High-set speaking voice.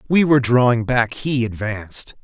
No: low, 120 Hz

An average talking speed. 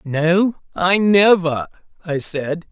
No: slow, 110 wpm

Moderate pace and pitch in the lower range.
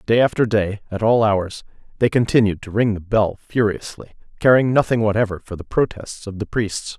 Yes: average, 180 wpm; low, 110 Hz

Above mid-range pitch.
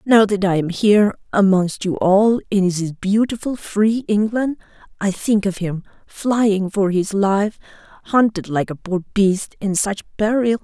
Yes: high, 200 Hz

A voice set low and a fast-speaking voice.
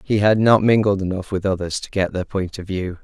Yes: low, 100 Hz; fast, 255 wpm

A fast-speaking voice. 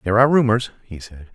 Yes: fast, 225 wpm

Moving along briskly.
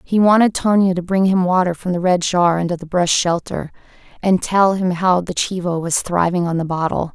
Yes: fast, 220 wpm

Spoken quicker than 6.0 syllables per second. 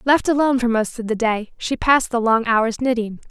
No: 5.5 syllables/s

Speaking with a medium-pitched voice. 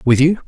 Yes: medium, 150 Hz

